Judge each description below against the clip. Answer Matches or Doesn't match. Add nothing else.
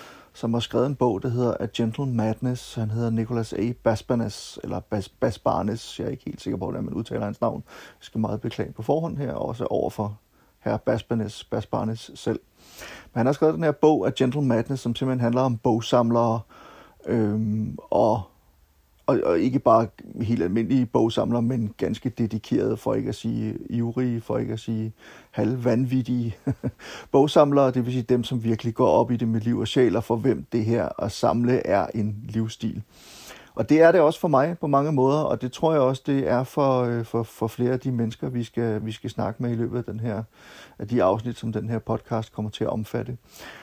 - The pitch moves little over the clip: Matches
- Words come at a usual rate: Matches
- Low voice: Matches